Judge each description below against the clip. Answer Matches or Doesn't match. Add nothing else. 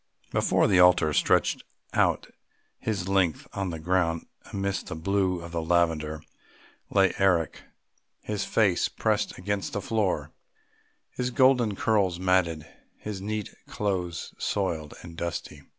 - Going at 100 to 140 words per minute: Matches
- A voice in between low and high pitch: Doesn't match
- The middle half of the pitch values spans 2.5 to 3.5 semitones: Matches